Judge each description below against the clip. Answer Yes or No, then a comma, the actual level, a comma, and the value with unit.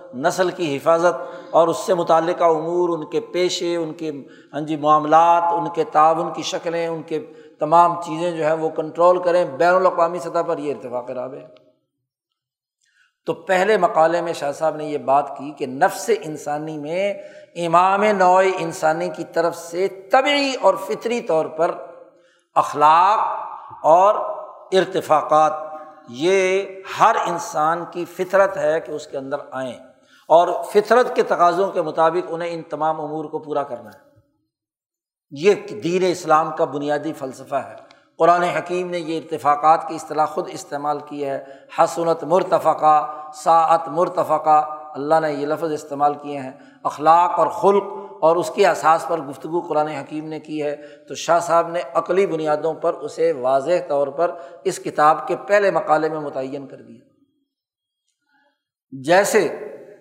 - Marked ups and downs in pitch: No, narrow, 2.5 semitones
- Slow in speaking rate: No, average, 155 wpm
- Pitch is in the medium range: Yes, medium, 165 Hz